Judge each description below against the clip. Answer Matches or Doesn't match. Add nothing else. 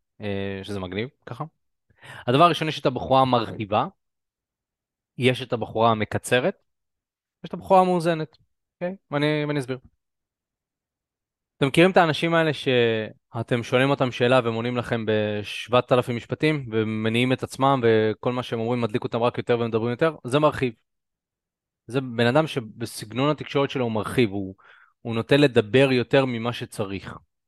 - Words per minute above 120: Matches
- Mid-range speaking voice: Doesn't match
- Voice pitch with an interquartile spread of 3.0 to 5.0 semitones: Matches